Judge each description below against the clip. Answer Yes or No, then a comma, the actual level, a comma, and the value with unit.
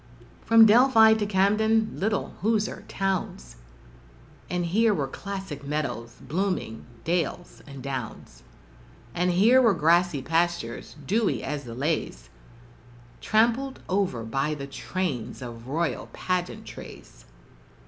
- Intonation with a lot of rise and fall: Yes, wide, 7.2 semitones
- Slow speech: Yes, slow, 110 wpm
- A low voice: No, medium, 175 Hz